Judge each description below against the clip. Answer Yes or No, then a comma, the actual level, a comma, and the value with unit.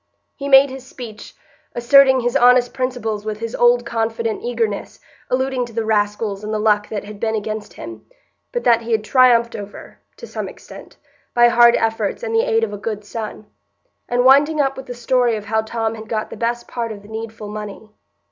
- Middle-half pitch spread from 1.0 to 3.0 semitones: Yes, average, 2.7 semitones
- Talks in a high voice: Yes, high, 230 Hz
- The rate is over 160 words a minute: Yes, fast, 205 wpm